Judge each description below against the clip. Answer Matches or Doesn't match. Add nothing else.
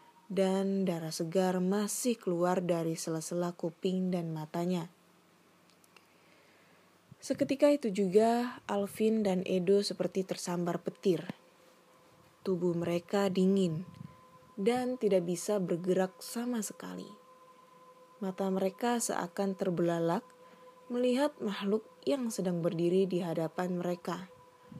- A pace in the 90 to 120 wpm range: Matches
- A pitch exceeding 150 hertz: Matches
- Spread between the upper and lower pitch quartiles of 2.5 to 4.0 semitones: Matches